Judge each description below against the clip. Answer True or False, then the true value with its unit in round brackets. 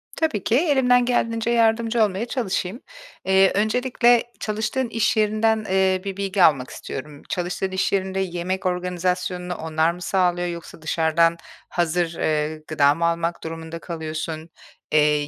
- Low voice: False (185 Hz)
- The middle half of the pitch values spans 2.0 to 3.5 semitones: False (4.6 semitones)